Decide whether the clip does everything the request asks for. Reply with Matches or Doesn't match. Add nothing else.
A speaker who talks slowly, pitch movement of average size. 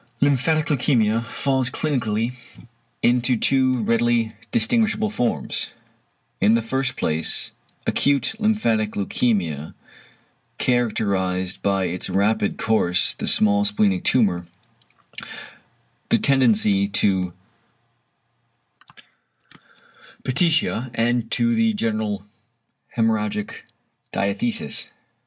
Matches